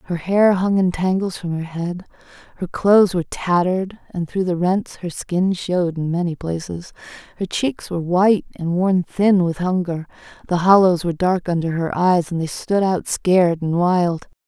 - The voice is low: No, medium, 180 Hz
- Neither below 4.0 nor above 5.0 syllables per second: Yes, 4.8 syllables/s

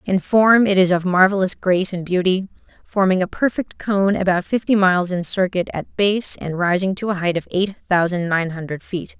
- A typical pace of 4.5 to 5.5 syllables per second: Yes, 5.1 syllables/s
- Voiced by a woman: Yes, female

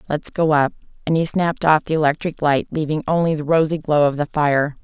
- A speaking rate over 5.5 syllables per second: Yes, 5.7 syllables/s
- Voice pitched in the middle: Yes, medium, 155 Hz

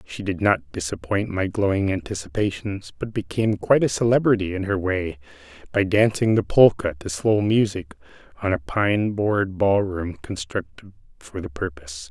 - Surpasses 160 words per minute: No, average, 155 wpm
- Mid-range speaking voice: No, low, 105 Hz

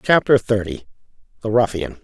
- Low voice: Yes, low, 120 Hz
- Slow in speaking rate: Yes, slow, 90 wpm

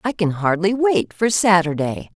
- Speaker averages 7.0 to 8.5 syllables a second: No, 4.4 syllables/s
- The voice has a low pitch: No, medium, 185 Hz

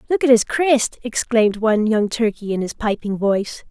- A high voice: Yes, high, 225 Hz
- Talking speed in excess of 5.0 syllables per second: Yes, 5.2 syllables/s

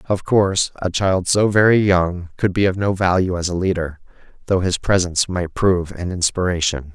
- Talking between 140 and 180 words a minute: No, average, 190 wpm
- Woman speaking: No, male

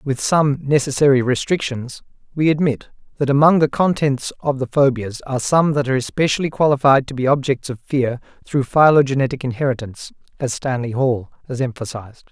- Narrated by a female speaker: No, male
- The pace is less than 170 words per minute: Yes, average, 155 wpm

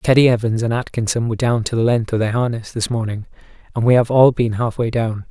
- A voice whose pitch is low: Yes, low, 115 Hz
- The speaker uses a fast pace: Yes, fast, 240 wpm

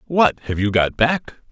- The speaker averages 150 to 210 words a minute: Yes, average, 200 wpm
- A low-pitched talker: Yes, low, 130 Hz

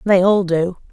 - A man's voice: No, female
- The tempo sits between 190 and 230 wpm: Yes, average, 195 wpm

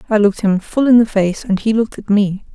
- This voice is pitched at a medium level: No, high, 210 Hz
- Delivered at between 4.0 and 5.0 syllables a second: No, 6.1 syllables/s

